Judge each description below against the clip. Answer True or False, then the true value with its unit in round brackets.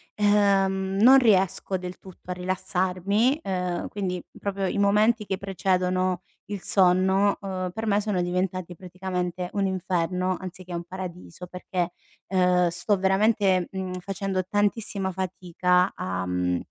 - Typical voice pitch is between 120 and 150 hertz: False (185 Hz)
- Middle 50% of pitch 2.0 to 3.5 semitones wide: False (1.5 semitones)